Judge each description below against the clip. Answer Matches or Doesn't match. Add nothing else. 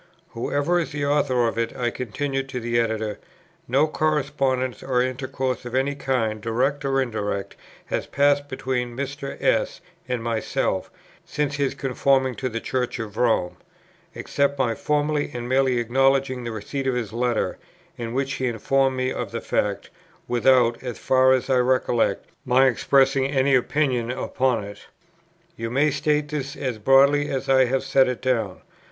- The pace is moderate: Matches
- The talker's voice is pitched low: Matches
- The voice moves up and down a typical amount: Doesn't match